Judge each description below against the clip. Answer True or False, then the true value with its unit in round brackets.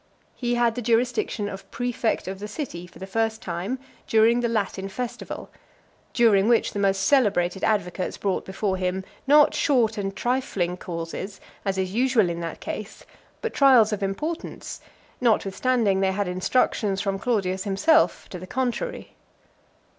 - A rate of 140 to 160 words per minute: True (155 wpm)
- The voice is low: False (210 Hz)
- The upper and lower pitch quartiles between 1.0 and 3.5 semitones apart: False (4.1 semitones)